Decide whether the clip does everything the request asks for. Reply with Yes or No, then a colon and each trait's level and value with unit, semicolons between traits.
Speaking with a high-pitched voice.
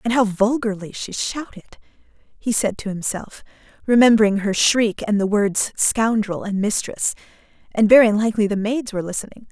Yes: high, 215 Hz